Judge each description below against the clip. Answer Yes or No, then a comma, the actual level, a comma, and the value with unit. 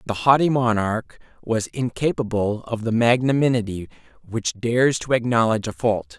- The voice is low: Yes, low, 115 Hz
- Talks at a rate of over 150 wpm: No, average, 145 wpm